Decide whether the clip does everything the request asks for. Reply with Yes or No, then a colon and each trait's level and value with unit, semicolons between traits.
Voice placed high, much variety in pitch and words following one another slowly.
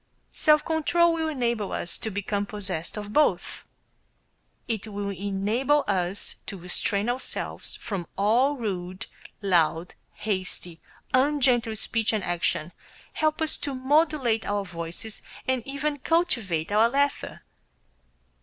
Yes: high, 220 Hz; wide, 6.0 semitones; slow, 120 wpm